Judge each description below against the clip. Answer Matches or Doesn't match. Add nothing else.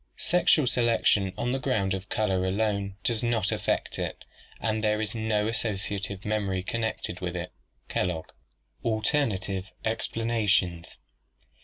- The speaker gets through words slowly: Matches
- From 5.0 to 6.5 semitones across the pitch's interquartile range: Doesn't match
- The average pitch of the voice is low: Matches